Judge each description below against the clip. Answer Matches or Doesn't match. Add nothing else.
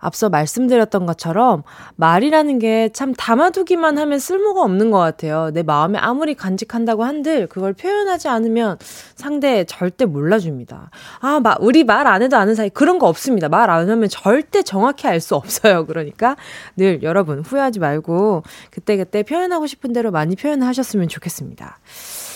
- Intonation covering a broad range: Matches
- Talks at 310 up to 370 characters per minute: Matches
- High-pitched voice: Matches